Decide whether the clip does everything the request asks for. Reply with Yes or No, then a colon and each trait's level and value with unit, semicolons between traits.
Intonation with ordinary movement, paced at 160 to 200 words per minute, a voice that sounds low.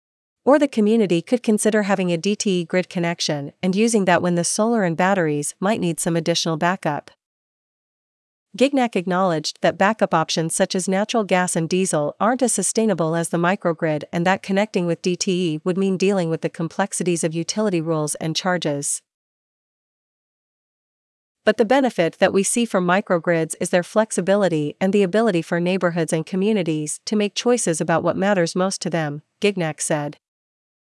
No: average, 3.3 semitones; average, 165 wpm; medium, 185 Hz